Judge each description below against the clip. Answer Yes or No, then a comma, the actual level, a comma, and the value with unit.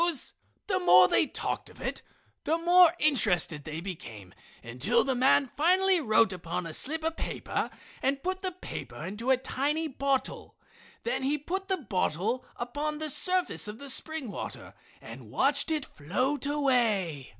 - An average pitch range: No, wide, 8.3 semitones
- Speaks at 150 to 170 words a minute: Yes, average, 160 wpm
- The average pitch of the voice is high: Yes, very high, 270 Hz